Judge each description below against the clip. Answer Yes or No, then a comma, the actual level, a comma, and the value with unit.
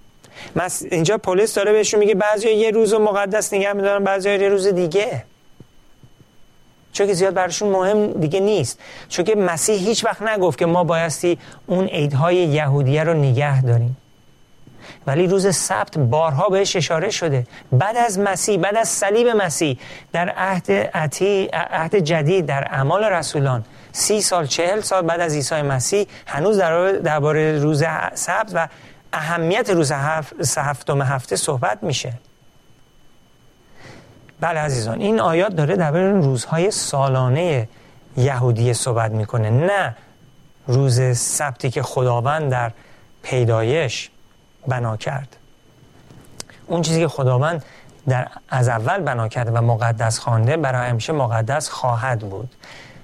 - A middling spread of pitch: No, wide, 6.6 semitones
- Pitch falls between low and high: Yes, medium, 155 Hz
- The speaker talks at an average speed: Yes, average, 130 wpm